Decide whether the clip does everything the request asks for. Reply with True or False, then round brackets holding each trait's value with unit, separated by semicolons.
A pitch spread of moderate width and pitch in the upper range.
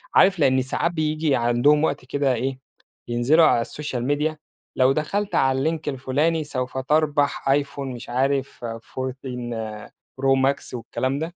False (3.1 semitones; 135 Hz)